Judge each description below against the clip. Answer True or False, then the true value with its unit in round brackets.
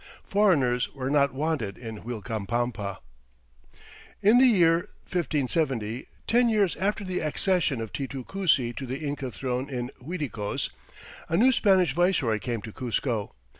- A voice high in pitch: False (135 Hz)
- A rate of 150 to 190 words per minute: False (135 wpm)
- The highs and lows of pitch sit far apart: True (7.0 semitones)